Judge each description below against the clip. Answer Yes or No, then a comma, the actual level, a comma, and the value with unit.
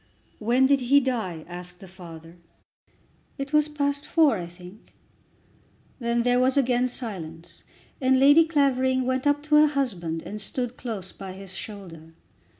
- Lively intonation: Yes, wide, 7.3 semitones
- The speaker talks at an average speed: Yes, average, 150 wpm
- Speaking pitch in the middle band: No, high, 240 Hz